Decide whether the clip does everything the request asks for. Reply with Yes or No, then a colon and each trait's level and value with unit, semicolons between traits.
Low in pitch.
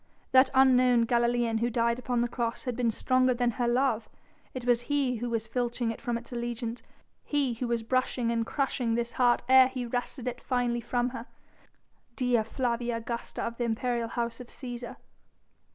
No: high, 240 Hz